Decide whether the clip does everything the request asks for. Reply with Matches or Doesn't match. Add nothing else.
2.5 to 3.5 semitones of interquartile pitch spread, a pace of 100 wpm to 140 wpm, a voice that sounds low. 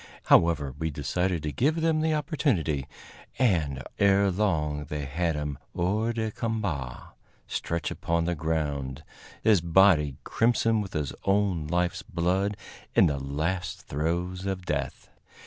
Doesn't match